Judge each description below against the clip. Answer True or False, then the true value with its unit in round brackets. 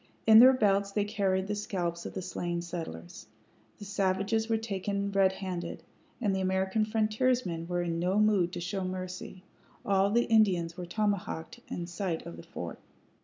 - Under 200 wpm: True (170 wpm)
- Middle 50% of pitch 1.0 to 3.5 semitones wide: True (3.0 semitones)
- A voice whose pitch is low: False (190 Hz)